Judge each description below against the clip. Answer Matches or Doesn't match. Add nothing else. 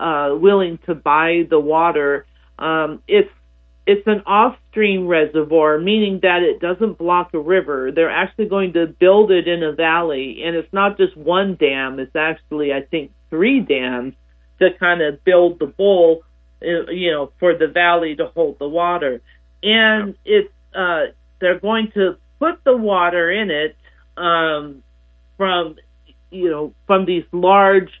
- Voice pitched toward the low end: Doesn't match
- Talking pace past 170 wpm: Doesn't match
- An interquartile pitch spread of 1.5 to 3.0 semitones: Doesn't match